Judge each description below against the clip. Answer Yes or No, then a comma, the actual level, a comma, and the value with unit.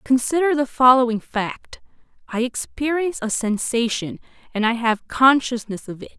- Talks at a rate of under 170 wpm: Yes, slow, 135 wpm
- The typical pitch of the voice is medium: No, high, 245 Hz